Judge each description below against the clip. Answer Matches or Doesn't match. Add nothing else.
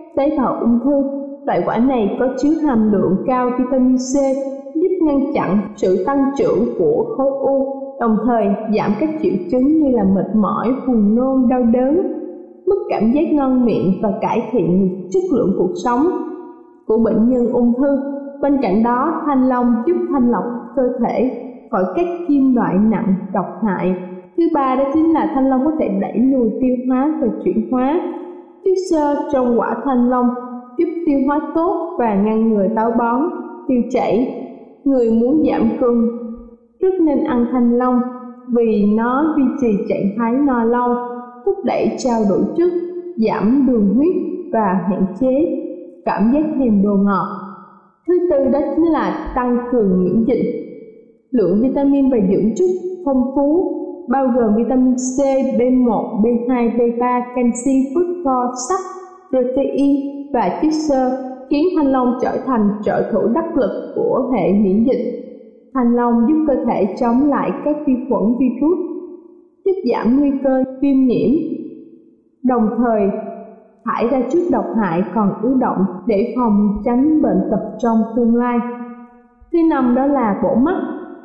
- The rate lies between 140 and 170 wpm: Matches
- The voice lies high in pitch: Matches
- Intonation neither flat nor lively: Matches